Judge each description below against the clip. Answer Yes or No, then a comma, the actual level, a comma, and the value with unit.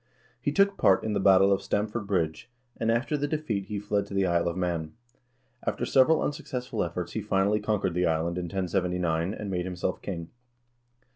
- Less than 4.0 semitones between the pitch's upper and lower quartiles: Yes, average, 3.6 semitones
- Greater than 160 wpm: Yes, average, 190 wpm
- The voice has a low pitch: Yes, very low, 95 Hz